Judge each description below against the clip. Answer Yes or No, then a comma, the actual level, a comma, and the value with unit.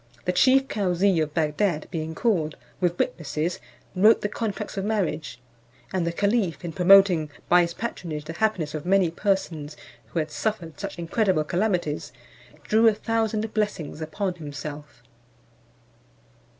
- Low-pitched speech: No, medium, 180 Hz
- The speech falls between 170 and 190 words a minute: No, average, 140 wpm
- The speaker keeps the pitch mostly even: No, average, 4.7 semitones